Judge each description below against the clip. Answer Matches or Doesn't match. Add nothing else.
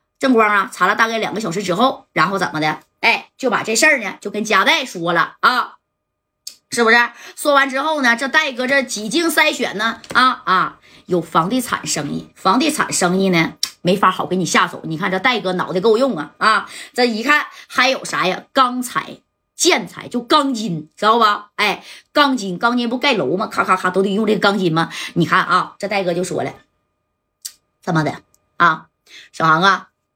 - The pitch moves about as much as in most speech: Doesn't match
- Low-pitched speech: Doesn't match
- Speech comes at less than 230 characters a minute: Doesn't match